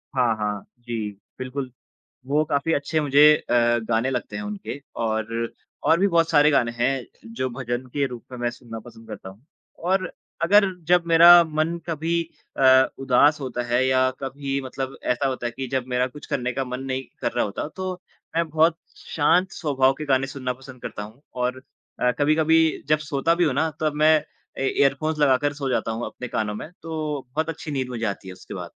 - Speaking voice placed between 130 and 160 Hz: Yes, low, 135 Hz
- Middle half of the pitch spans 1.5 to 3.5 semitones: No, average, 4.0 semitones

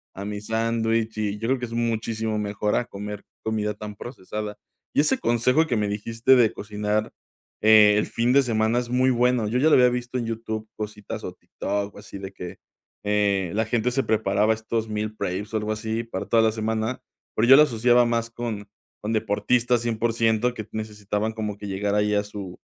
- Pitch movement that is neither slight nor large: No, narrow, 2.0 semitones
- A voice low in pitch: Yes, low, 110 Hz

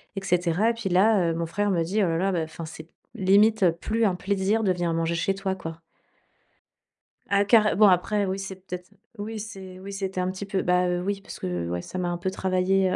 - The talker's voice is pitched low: No, high, 190 Hz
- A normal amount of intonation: No, narrow, 2.3 semitones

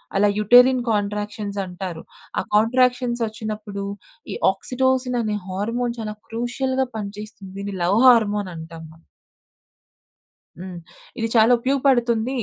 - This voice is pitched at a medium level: No, high, 215 Hz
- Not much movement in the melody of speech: No, average, 3.5 semitones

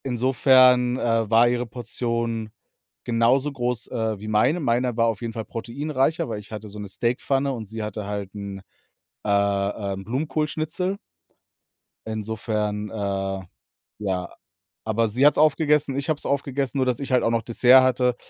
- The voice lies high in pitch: No, low, 115 Hz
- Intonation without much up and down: No, average, 3.7 semitones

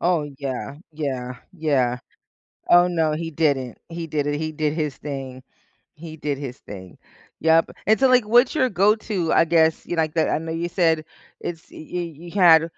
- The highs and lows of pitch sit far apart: No, average, 3.0 semitones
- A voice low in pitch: No, medium, 160 Hz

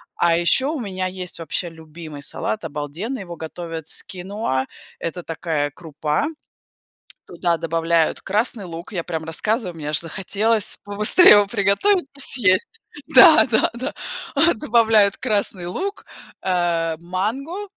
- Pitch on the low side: No, medium, 185 Hz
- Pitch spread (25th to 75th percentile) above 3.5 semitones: Yes, average, 5.1 semitones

